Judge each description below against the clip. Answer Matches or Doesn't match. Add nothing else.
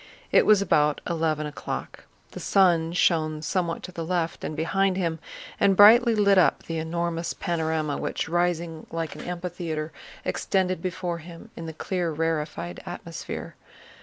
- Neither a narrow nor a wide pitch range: Doesn't match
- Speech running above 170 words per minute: Doesn't match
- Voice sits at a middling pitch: Matches